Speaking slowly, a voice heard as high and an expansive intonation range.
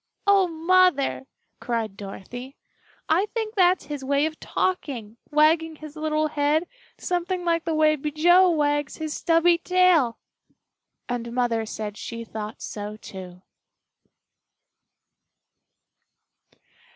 Yes: slow, 110 wpm; very high, 305 Hz; wide, 6.1 semitones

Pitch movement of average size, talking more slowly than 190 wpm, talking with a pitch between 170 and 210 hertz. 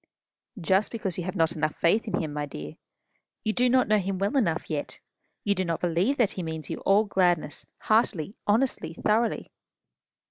No: average, 4.8 semitones; average, 200 wpm; medium, 185 Hz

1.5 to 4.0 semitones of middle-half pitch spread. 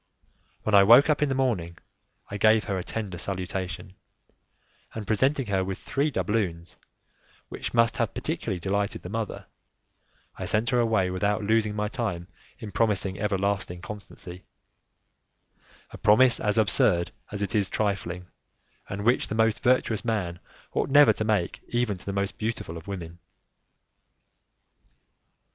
Yes: average, 3.2 semitones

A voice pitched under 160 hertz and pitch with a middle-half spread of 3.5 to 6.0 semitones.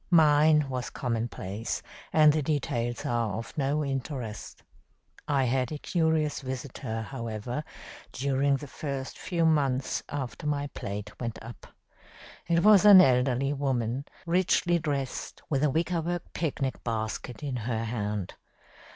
Yes: low, 135 Hz; average, 4.2 semitones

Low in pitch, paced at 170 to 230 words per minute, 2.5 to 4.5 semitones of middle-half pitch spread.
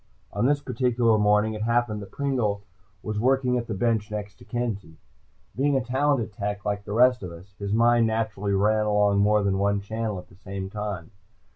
Yes: low, 105 Hz; average, 195 wpm; average, 2.8 semitones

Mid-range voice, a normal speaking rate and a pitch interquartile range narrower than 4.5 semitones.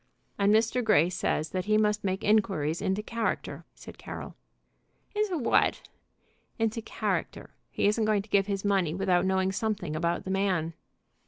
No: high, 200 Hz; average, 160 wpm; average, 2.7 semitones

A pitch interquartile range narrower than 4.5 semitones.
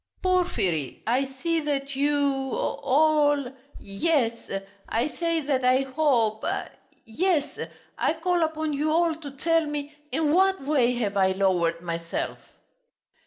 No: average, 4.8 semitones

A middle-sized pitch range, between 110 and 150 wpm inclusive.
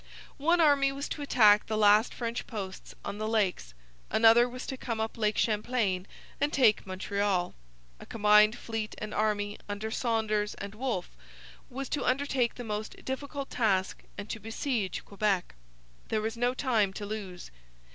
No: average, 3.2 semitones; average, 160 wpm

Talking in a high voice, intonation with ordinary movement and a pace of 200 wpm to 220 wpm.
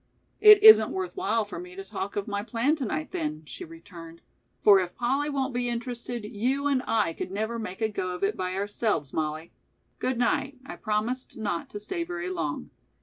No: high, 220 Hz; wide, 6.0 semitones; fast, 205 wpm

